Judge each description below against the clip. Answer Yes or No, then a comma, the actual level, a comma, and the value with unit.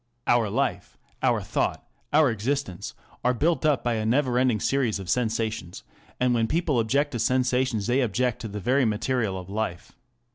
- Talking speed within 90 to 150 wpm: No, average, 175 wpm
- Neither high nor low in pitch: No, low, 120 Hz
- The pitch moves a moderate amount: Yes, average, 3.1 semitones